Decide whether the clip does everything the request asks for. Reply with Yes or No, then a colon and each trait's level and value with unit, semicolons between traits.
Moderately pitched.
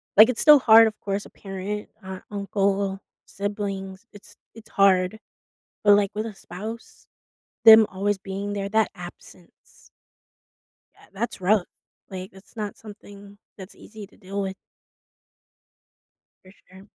No: high, 200 Hz